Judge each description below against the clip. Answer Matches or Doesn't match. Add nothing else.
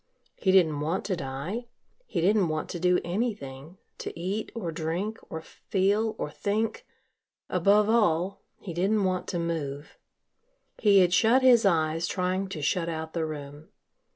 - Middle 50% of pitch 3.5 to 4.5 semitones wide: Matches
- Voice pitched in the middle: Matches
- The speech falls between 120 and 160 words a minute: Matches